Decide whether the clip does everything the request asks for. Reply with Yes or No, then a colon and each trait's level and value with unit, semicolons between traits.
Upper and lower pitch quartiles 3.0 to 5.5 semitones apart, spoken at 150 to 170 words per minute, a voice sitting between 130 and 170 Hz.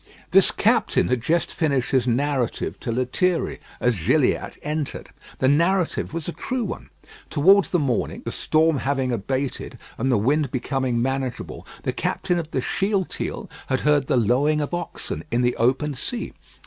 Yes: average, 4.2 semitones; average, 160 wpm; medium, 140 Hz